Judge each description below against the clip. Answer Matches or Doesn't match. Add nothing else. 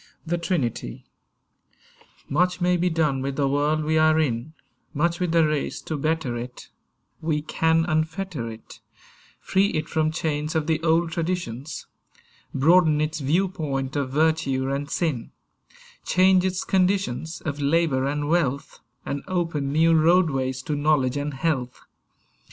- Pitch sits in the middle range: Matches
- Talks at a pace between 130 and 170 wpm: Matches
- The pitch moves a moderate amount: Matches